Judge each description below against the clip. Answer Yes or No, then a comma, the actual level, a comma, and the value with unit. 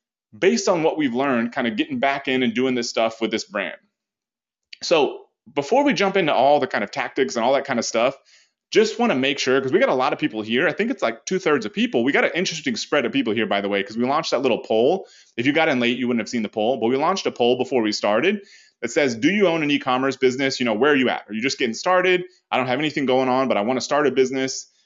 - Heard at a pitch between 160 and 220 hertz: No, low, 130 Hz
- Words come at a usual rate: No, fast, 295 wpm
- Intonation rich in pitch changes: Yes, wide, 7.0 semitones